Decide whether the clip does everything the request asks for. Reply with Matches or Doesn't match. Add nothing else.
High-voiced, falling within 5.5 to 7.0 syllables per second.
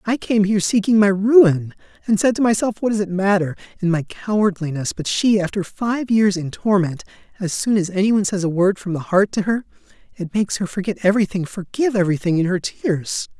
Matches